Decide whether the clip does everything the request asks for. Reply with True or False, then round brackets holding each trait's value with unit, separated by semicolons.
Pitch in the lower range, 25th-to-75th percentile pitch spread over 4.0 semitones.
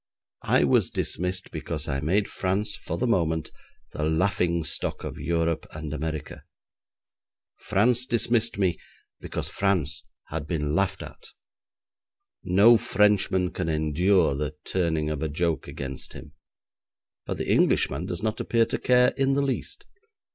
True (90 Hz; 4.8 semitones)